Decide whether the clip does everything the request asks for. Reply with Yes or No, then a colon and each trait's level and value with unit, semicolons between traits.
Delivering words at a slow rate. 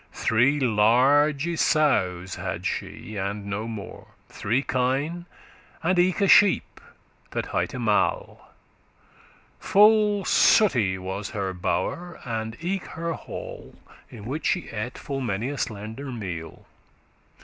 Yes: slow, 125 wpm